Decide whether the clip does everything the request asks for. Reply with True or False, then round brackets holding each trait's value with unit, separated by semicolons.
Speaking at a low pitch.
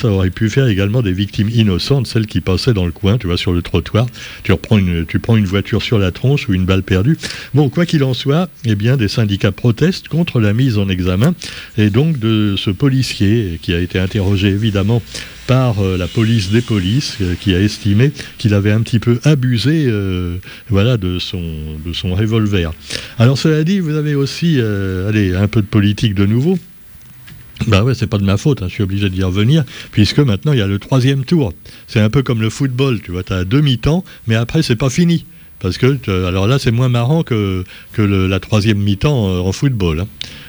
True (110 Hz)